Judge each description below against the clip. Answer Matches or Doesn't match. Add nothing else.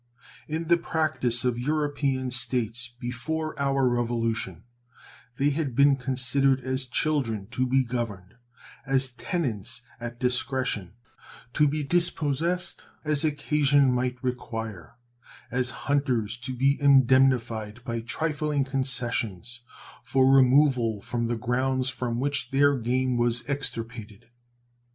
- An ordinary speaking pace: Doesn't match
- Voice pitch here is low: Matches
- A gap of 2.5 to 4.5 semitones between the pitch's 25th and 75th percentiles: Matches